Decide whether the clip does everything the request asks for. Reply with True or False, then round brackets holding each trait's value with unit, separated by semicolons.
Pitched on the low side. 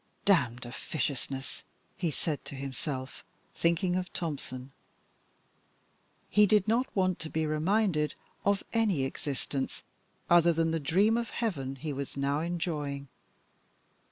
False (160 Hz)